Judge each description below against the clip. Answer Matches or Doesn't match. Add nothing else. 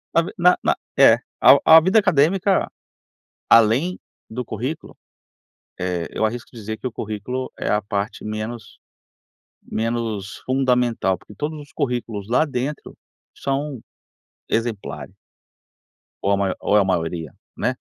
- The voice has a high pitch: Doesn't match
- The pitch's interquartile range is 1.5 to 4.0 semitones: Doesn't match